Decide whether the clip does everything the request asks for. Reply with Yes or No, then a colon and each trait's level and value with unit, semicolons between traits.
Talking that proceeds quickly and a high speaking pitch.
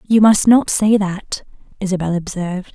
No: average, 155 wpm; high, 195 Hz